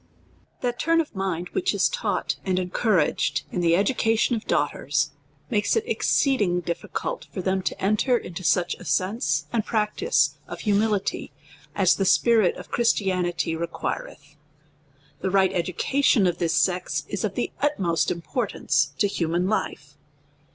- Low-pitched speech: No, high, 190 Hz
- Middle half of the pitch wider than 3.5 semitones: Yes, average, 4.5 semitones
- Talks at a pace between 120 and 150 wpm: No, average, 160 wpm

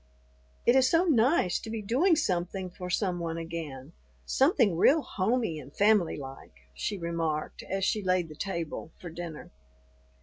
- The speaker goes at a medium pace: Yes, average, 160 wpm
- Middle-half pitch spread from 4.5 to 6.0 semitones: Yes, average, 5.1 semitones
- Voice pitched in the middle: Yes, medium, 180 Hz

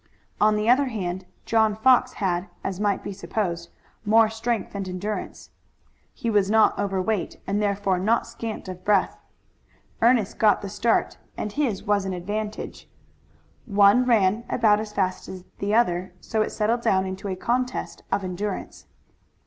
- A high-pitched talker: Yes, high, 205 Hz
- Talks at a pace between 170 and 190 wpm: No, average, 160 wpm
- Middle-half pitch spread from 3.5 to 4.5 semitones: No, average, 2.7 semitones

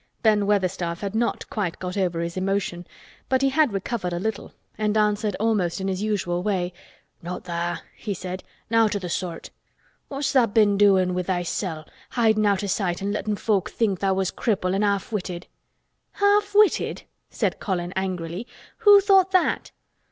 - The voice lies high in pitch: Yes, high, 200 Hz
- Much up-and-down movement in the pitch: No, average, 3.3 semitones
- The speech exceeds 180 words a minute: No, average, 170 wpm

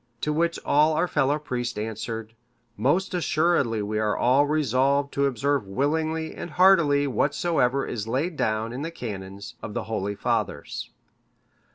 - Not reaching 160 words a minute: Yes, average, 150 wpm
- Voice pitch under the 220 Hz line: Yes, medium, 140 Hz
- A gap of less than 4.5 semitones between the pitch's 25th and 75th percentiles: No, wide, 5.6 semitones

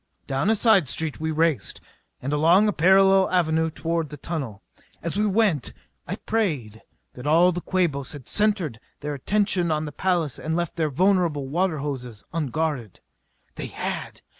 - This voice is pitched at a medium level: Yes, medium, 160 Hz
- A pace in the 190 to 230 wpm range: No, average, 165 wpm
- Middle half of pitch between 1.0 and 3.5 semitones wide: No, average, 4.3 semitones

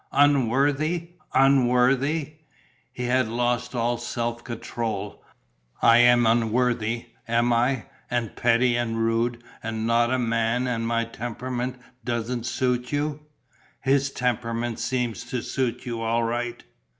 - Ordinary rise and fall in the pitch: No, narrow, 1.6 semitones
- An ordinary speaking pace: No, slow, 125 wpm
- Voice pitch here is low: Yes, low, 120 Hz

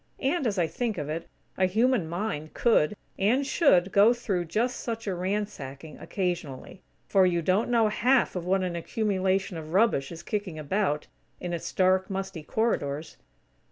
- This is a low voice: No, high, 190 Hz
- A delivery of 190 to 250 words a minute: No, average, 165 wpm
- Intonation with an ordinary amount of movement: Yes, average, 4.3 semitones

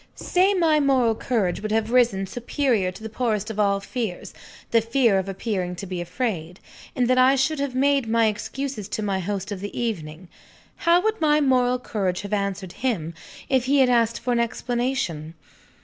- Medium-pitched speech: No, high, 225 Hz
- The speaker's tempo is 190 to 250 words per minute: Yes, average, 195 wpm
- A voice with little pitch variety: No, average, 4.8 semitones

